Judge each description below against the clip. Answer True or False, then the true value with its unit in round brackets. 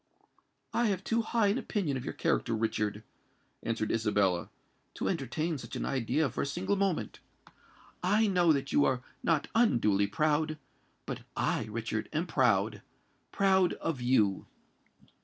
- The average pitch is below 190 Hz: True (140 Hz)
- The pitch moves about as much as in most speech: False (8.3 semitones)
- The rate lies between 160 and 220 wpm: False (140 wpm)